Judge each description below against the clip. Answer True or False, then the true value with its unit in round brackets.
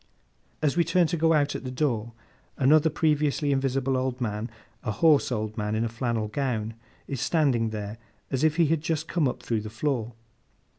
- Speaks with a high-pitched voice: False (135 Hz)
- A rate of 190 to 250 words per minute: True (195 wpm)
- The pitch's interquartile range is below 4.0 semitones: False (5.0 semitones)